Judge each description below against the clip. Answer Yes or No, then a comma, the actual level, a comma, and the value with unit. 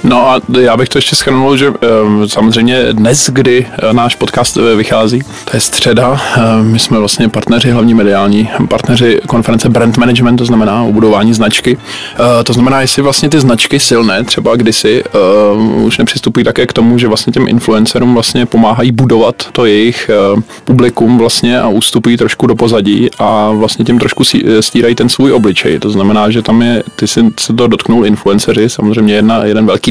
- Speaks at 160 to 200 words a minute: Yes, fast, 170 wpm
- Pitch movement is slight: Yes, narrow, 2.0 semitones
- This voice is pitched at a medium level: No, low, 115 Hz